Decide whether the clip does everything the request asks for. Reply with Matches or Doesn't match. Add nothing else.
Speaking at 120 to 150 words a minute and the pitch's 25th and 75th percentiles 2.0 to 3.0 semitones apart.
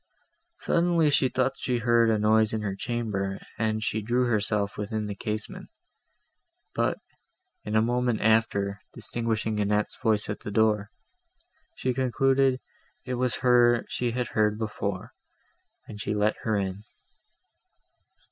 Matches